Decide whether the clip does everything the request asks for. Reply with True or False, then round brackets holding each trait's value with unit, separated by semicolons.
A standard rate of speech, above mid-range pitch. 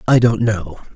False (190 wpm; 110 Hz)